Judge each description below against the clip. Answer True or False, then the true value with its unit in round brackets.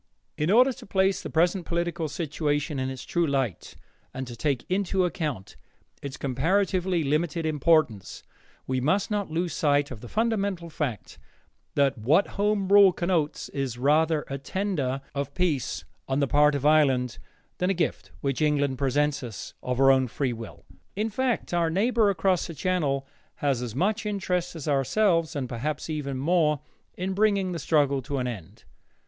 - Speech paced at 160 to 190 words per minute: True (170 wpm)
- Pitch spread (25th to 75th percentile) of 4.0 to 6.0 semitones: True (5.1 semitones)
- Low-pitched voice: False (155 Hz)